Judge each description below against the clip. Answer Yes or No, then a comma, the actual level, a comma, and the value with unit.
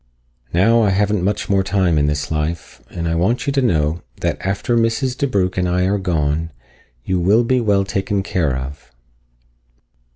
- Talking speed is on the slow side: No, average, 175 wpm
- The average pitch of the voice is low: Yes, very low, 95 Hz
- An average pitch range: Yes, average, 4.1 semitones